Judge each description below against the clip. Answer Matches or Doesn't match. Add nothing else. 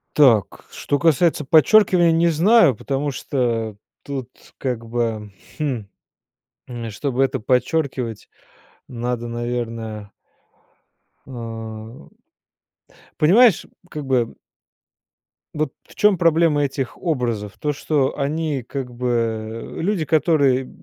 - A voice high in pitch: Doesn't match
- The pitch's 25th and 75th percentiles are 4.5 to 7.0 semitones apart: Matches